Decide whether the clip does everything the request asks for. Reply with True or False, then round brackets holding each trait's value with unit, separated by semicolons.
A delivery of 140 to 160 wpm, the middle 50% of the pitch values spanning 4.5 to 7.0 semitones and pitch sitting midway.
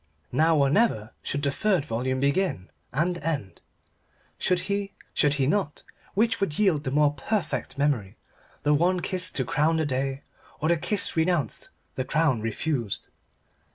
True (155 wpm; 4.8 semitones; 150 Hz)